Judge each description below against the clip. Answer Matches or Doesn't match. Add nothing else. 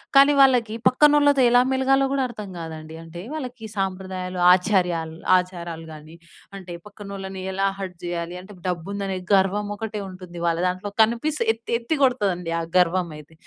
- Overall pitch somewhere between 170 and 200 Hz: Matches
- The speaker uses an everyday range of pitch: Matches